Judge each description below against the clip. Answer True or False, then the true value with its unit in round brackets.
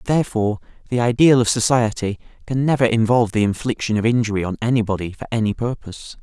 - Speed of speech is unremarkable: True (165 wpm)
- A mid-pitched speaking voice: False (115 Hz)